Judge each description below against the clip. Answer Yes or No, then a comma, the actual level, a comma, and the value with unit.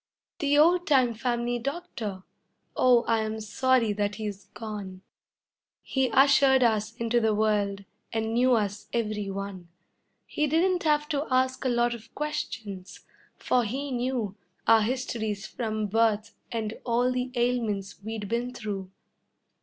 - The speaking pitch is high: Yes, high, 230 Hz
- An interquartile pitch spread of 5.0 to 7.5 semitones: No, average, 3.4 semitones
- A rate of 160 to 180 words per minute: No, average, 140 wpm